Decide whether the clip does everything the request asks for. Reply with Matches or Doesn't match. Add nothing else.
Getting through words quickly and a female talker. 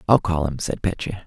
Doesn't match